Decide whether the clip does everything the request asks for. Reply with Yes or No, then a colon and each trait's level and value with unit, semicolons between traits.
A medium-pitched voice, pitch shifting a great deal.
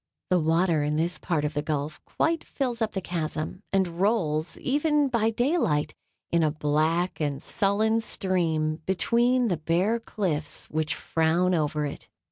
Yes: medium, 170 Hz; wide, 6.0 semitones